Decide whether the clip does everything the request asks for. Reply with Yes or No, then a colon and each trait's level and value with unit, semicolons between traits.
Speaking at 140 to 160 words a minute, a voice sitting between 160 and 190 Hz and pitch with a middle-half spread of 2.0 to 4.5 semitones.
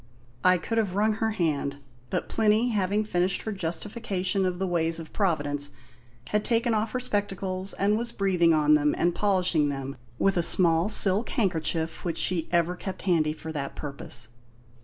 No: average, 175 wpm; medium, 185 Hz; average, 4.2 semitones